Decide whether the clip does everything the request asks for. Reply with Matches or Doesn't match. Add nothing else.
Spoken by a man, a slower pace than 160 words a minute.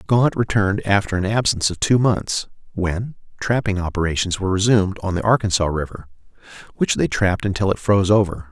Doesn't match